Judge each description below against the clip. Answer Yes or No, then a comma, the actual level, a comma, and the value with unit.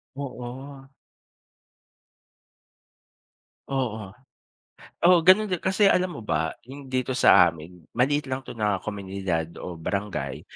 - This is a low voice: Yes, low, 125 Hz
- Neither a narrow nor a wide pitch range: No, wide, 6.4 semitones